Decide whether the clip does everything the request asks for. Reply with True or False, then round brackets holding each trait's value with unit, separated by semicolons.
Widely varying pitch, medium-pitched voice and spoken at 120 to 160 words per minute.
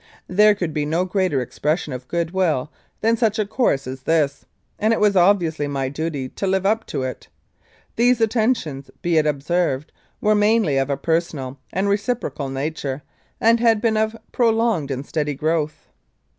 False (6.8 semitones; 170 Hz; 170 wpm)